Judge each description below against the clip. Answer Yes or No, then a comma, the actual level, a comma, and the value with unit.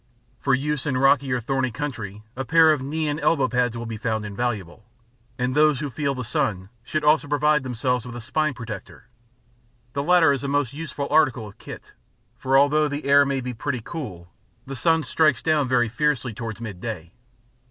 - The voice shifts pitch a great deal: No, average, 3.8 semitones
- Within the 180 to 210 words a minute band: Yes, average, 195 wpm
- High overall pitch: No, low, 135 Hz